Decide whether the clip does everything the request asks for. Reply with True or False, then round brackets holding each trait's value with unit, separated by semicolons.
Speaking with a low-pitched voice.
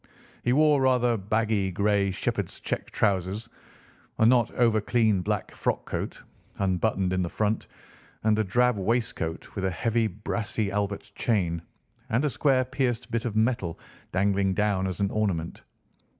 True (105 Hz)